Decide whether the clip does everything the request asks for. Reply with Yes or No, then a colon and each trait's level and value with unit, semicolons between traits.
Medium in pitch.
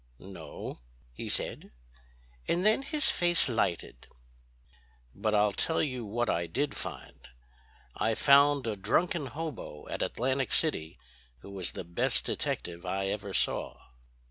No: low, 115 Hz